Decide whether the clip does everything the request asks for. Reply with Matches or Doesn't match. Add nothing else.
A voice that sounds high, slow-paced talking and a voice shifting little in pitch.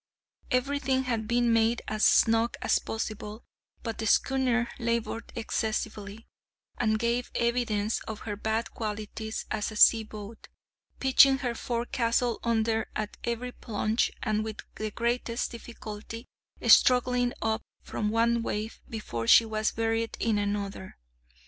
Matches